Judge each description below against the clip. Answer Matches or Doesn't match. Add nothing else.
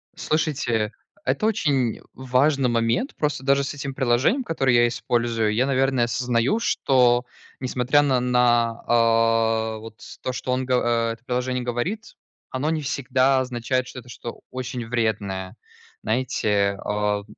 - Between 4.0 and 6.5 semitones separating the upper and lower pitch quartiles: Doesn't match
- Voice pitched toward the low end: Matches